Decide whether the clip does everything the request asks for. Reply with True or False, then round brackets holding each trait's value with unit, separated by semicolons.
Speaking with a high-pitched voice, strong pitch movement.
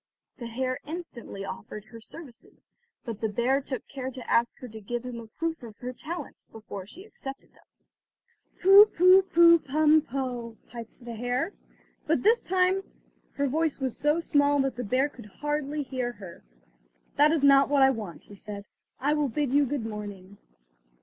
False (265 Hz; 4.5 semitones)